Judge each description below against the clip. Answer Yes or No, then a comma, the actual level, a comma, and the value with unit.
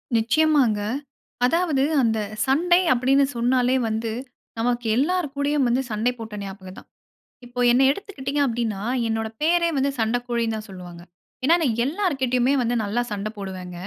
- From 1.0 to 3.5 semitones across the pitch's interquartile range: No, average, 4.2 semitones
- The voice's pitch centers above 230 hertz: Yes, high, 245 Hz